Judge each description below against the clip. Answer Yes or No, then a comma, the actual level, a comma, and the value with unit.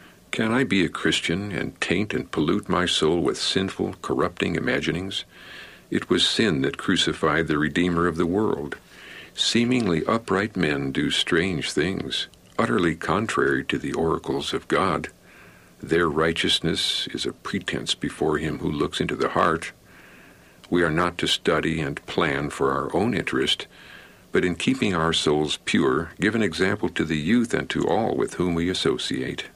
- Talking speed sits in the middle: Yes, average, 160 wpm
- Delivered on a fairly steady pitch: No, average, 3.4 semitones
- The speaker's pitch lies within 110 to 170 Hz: No, very low, 85 Hz